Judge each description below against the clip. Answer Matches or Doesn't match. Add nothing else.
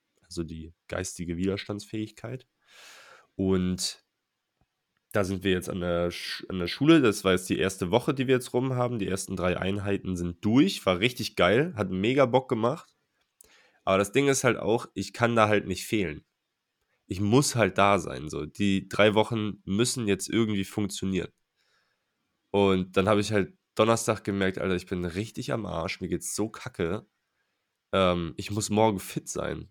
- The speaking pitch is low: Matches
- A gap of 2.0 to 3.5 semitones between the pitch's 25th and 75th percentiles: Matches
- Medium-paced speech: Matches